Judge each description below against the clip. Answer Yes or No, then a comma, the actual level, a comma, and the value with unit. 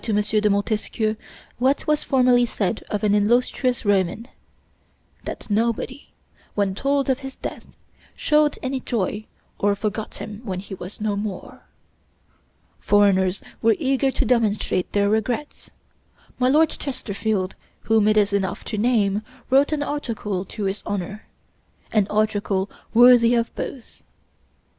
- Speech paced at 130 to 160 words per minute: Yes, slow, 135 wpm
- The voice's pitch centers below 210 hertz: No, high, 215 Hz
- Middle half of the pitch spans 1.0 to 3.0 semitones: No, average, 3.6 semitones